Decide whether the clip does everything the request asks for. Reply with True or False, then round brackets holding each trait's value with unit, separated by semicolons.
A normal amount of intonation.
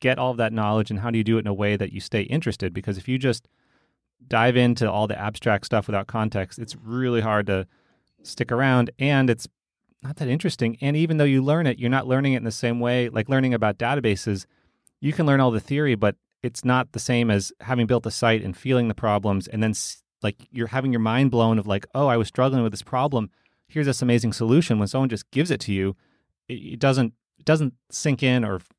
True (3.4 semitones)